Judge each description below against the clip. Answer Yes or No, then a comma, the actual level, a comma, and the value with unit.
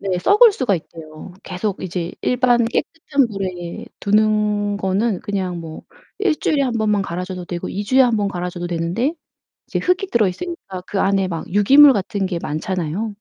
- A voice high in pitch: Yes, high, 200 Hz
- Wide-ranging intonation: No, average, 4.7 semitones